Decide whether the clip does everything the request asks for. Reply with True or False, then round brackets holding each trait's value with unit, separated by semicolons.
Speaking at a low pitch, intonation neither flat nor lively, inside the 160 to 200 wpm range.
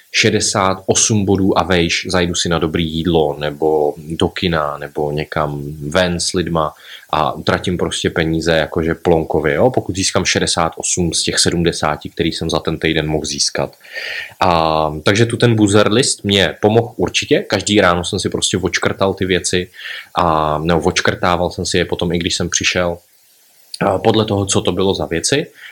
True (90 Hz; 3.6 semitones; 170 wpm)